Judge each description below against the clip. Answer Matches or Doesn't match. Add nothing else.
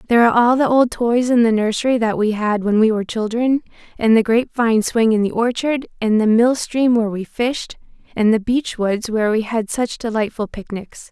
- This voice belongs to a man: Doesn't match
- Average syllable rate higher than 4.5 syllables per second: Matches